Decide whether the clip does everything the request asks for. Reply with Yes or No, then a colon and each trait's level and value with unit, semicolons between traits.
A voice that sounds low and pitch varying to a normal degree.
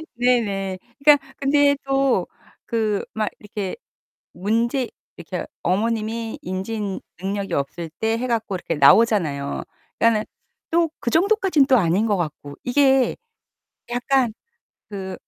No: high, 225 Hz; average, 4.9 semitones